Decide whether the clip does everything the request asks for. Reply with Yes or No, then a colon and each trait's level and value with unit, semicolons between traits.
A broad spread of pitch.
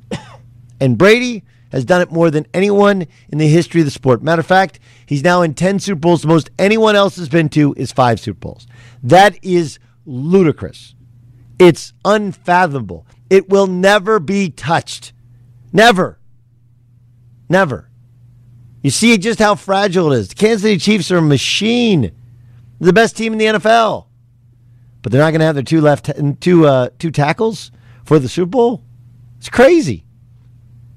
Yes: wide, 7.7 semitones